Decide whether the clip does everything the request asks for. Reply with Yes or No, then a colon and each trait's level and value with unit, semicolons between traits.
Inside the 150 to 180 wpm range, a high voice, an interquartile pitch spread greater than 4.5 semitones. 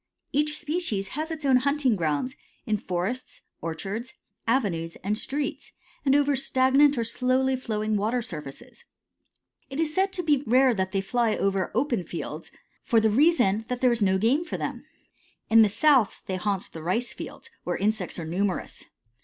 Yes: average, 170 wpm; high, 230 Hz; wide, 5.6 semitones